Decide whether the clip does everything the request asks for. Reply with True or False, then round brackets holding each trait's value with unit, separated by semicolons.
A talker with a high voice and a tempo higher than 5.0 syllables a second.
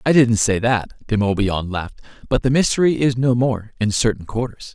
False (115 Hz; 5.4 syllables/s)